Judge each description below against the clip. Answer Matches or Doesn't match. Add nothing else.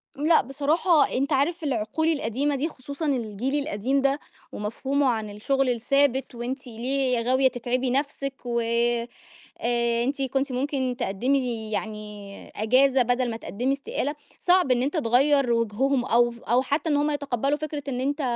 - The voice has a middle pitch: Doesn't match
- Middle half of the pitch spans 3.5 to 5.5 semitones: Doesn't match